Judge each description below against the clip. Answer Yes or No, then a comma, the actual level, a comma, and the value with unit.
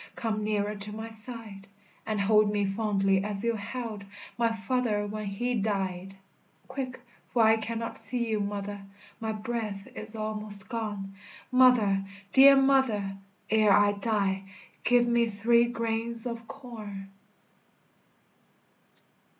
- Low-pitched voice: No, high, 215 Hz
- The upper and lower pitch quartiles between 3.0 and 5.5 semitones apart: No, narrow, 2.5 semitones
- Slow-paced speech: Yes, slow, 125 wpm